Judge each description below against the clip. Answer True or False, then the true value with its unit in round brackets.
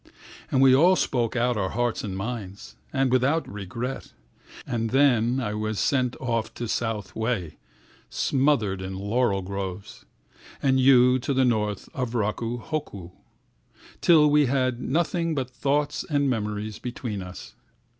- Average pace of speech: False (130 wpm)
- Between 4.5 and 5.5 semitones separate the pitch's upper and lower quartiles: False (4.1 semitones)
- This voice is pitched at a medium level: False (120 Hz)